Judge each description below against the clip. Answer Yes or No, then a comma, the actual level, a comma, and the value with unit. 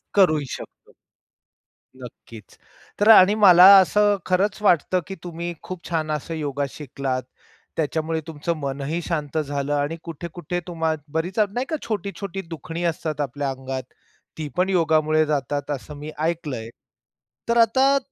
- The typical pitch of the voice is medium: Yes, medium, 160 Hz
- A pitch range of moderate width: Yes, average, 4.0 semitones